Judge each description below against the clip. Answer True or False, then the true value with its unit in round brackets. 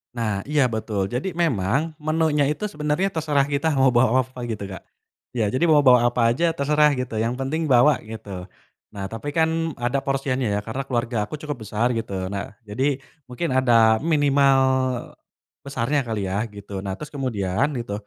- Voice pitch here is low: True (130 Hz)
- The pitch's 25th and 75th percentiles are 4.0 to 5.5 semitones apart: True (4.9 semitones)